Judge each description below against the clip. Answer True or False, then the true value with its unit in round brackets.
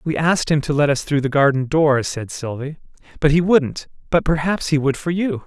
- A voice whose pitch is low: False (150 Hz)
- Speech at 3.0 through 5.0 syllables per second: False (5.3 syllables/s)